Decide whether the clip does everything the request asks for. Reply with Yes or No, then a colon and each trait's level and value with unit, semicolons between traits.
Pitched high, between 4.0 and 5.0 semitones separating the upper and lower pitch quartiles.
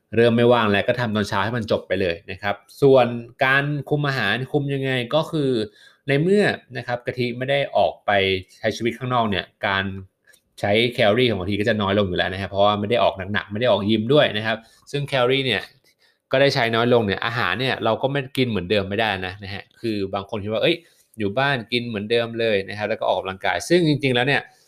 No: low, 115 Hz; average, 4.5 semitones